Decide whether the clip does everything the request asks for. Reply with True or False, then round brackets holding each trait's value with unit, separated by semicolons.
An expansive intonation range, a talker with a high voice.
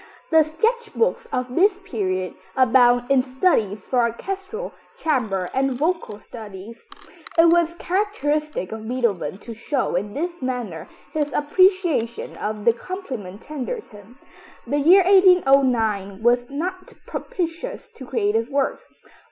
True (7.6 semitones; 265 Hz)